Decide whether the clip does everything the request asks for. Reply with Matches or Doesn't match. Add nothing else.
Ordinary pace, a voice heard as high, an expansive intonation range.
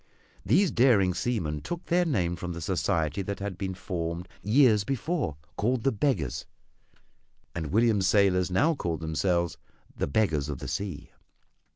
Doesn't match